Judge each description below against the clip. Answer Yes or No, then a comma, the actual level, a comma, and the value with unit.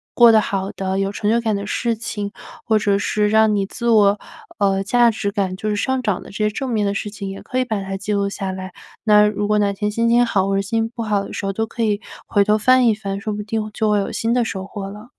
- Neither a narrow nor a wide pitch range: No, narrow, 2.0 semitones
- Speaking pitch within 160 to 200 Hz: No, high, 210 Hz